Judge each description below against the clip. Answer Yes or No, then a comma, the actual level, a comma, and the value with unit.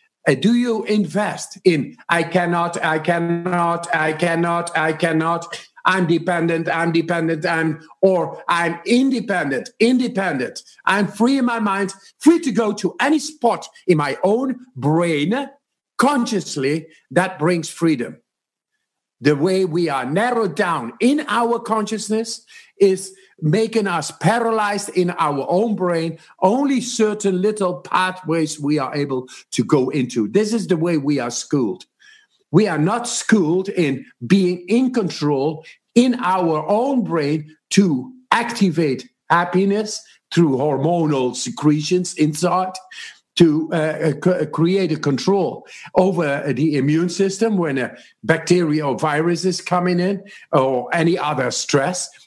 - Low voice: No, medium, 180 Hz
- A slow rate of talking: Yes, slow, 130 wpm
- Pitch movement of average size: Yes, average, 5.0 semitones